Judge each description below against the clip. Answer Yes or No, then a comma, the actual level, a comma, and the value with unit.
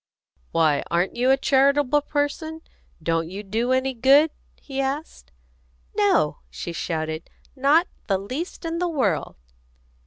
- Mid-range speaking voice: No, very high, 265 Hz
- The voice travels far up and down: Yes, wide, 8.3 semitones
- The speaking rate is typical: No, slow, 130 wpm